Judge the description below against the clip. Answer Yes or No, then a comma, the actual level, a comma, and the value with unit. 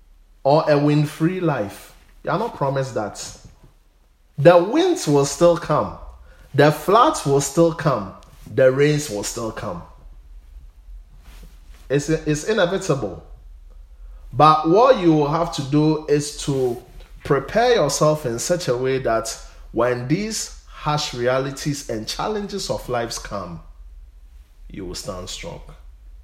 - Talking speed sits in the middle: No, slow, 130 wpm